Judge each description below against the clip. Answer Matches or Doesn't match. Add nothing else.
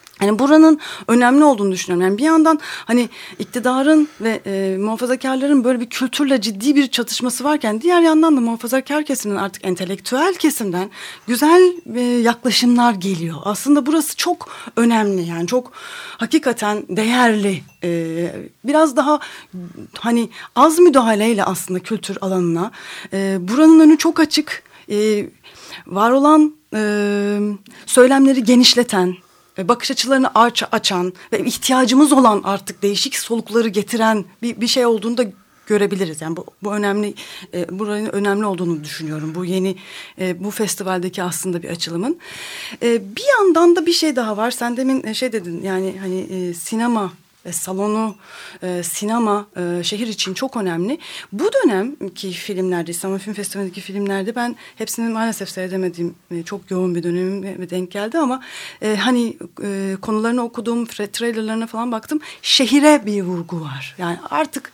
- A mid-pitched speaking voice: Doesn't match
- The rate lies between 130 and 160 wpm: Matches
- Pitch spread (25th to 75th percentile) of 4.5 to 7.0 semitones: Matches